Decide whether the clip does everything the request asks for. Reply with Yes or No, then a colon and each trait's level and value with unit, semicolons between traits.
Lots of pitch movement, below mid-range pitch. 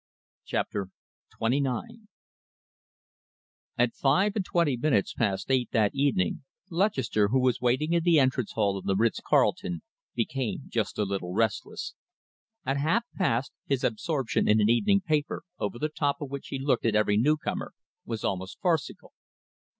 Yes: wide, 5.9 semitones; low, 130 Hz